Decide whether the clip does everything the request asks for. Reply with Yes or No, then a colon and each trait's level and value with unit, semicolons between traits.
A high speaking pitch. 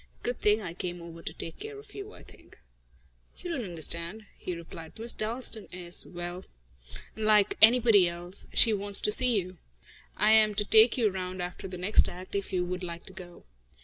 Yes: high, 195 Hz